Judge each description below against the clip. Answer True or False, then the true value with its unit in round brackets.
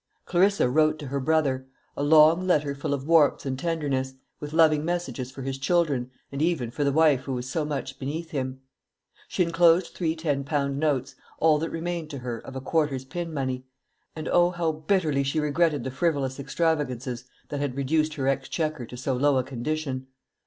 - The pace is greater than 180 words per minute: True (190 wpm)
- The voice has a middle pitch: True (145 Hz)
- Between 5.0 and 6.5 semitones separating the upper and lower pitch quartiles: False (3.3 semitones)